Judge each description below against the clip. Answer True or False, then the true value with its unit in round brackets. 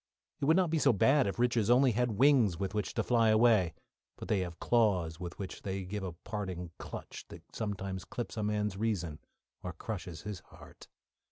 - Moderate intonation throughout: True (4.3 semitones)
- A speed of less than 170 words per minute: False (195 wpm)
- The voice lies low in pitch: True (105 Hz)